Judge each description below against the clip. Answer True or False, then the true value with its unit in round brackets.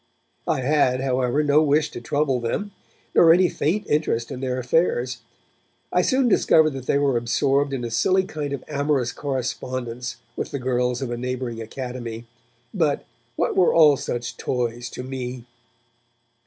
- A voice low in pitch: True (130 Hz)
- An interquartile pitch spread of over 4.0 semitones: False (3.3 semitones)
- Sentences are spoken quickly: False (160 wpm)